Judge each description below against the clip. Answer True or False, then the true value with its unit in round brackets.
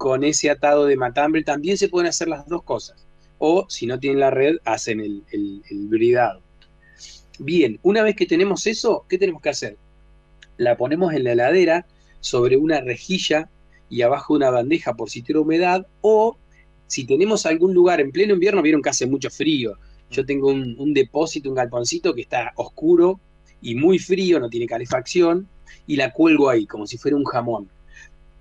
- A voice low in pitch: False (170 Hz)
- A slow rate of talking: False (185 wpm)